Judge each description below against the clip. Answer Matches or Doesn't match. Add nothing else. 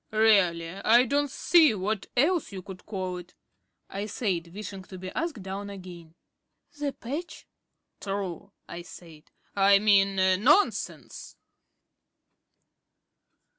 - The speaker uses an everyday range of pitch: Matches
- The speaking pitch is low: Doesn't match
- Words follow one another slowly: Matches